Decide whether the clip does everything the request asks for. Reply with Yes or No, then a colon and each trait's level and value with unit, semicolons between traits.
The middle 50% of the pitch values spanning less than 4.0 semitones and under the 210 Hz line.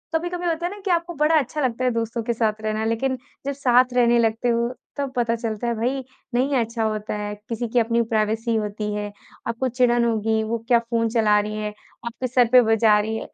No: narrow, 2.4 semitones; high, 235 Hz